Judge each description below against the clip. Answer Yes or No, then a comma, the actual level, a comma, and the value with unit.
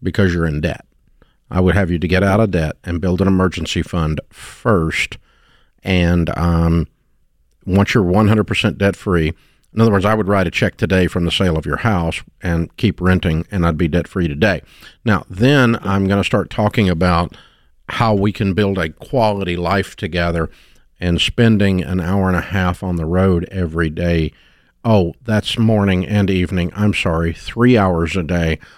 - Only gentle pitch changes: No, average, 3.3 semitones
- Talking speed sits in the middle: Yes, average, 185 wpm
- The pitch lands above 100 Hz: No, very low, 90 Hz